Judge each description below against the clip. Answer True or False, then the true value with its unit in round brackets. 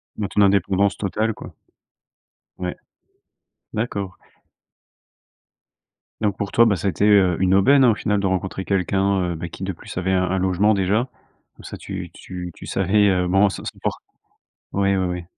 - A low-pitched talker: True (95 Hz)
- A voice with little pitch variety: True (1.8 semitones)